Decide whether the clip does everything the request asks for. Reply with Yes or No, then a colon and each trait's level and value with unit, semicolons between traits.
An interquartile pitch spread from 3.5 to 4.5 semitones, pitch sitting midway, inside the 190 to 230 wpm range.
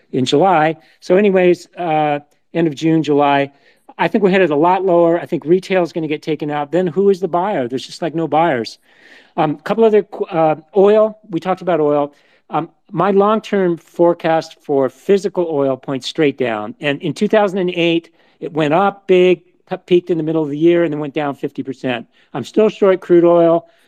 Yes: average, 3.8 semitones; medium, 170 Hz; average, 200 wpm